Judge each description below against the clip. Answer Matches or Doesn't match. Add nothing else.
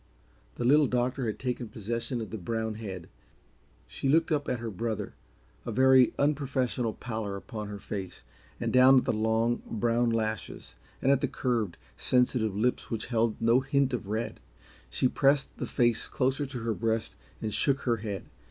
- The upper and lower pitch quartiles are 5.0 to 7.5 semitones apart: Doesn't match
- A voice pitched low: Matches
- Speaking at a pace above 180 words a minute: Doesn't match